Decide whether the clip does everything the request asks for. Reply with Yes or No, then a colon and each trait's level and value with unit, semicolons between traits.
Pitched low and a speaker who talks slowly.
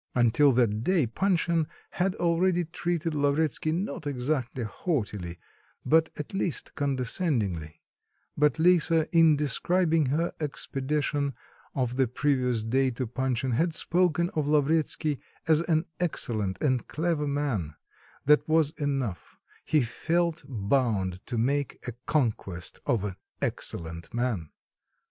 No: medium, 145 Hz; slow, 120 wpm